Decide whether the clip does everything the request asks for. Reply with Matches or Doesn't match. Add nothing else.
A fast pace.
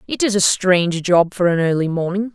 Matches